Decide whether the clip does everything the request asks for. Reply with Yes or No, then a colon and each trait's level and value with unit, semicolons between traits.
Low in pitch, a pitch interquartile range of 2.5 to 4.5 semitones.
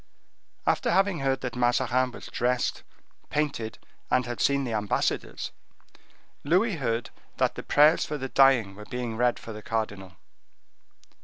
Yes: low, 125 Hz; average, 3.5 semitones